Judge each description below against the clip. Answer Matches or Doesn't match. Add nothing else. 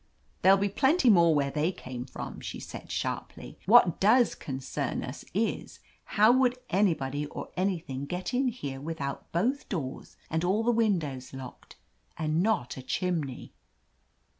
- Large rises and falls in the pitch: Matches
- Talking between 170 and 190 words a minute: Doesn't match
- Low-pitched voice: Doesn't match